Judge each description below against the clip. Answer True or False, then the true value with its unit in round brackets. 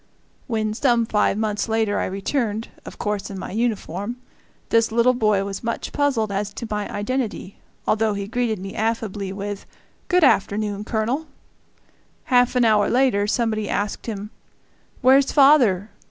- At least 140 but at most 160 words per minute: True (150 wpm)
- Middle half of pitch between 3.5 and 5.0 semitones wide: False (2.8 semitones)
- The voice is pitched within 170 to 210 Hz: False (220 Hz)